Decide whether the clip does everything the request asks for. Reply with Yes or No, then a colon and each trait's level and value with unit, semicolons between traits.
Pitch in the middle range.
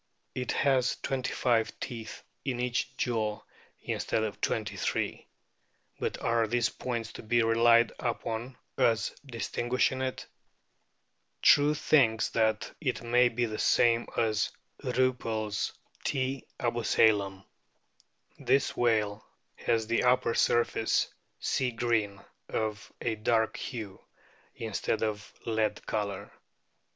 No: low, 115 Hz